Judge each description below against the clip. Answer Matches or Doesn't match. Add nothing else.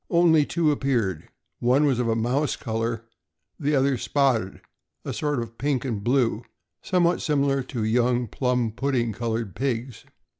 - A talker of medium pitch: Doesn't match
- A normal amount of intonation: Matches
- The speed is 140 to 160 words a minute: Matches